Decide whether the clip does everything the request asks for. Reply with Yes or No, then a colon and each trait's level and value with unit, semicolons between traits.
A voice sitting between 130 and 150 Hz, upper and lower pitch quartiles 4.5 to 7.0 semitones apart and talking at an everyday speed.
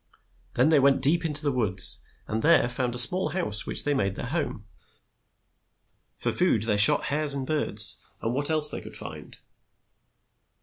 Yes: low, 135 Hz; wide, 5.4 semitones; average, 175 wpm